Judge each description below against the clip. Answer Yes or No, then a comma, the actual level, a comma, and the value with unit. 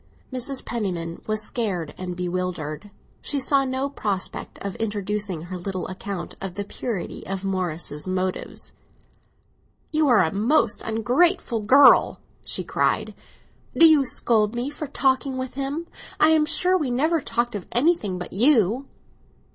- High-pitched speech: Yes, high, 220 Hz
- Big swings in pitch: Yes, wide, 6.6 semitones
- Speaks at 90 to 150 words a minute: Yes, average, 145 wpm